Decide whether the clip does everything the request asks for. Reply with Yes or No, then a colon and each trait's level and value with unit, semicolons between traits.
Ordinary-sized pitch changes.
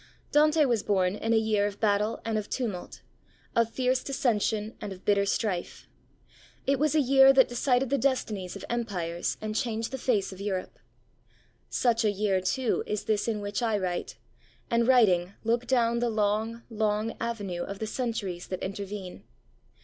Yes: average, 3.2 semitones